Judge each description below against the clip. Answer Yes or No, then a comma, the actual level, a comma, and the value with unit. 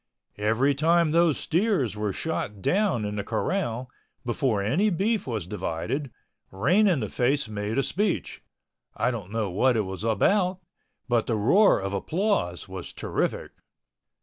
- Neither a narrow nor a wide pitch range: No, wide, 8.5 semitones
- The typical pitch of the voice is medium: No, low, 125 Hz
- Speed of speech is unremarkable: Yes, average, 150 wpm